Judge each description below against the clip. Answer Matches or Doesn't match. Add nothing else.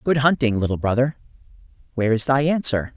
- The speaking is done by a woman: Doesn't match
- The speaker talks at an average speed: Matches